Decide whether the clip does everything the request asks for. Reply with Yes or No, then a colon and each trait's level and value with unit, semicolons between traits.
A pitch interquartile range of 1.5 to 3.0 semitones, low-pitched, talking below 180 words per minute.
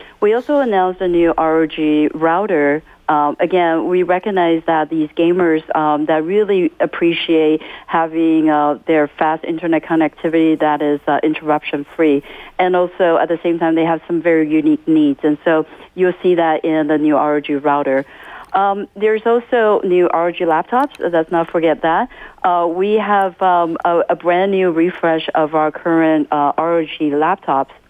No: narrow, 2.6 semitones; medium, 165 Hz; average, 165 wpm